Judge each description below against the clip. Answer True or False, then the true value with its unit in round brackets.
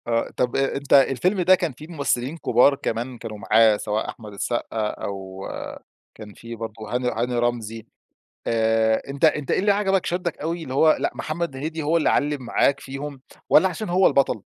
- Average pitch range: False (5.8 semitones)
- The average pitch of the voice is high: False (135 Hz)